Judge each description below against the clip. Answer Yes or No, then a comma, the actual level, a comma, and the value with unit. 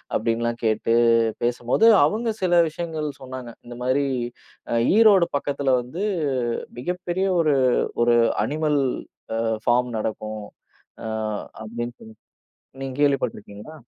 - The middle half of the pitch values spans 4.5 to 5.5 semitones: Yes, average, 5.1 semitones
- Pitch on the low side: Yes, low, 130 Hz